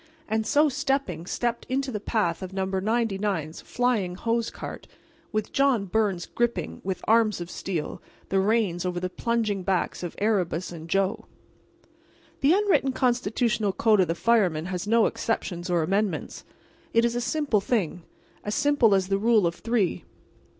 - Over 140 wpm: Yes, average, 155 wpm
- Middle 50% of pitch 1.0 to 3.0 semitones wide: No, average, 4.3 semitones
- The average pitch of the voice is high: Yes, high, 210 Hz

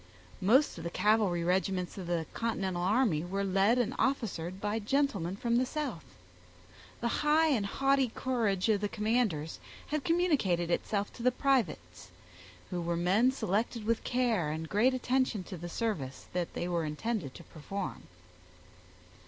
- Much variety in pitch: Yes, wide, 6.0 semitones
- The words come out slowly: No, average, 155 wpm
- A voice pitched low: No, high, 205 Hz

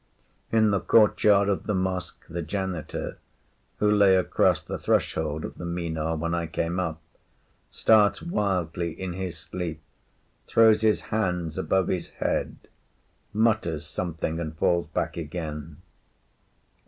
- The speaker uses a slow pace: Yes, slow, 130 wpm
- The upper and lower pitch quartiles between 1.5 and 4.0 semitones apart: Yes, average, 3.7 semitones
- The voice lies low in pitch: Yes, very low, 90 Hz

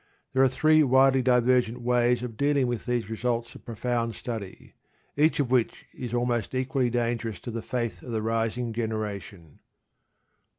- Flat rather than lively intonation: Yes, narrow, 2.0 semitones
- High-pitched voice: No, low, 120 Hz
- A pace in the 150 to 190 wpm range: Yes, average, 160 wpm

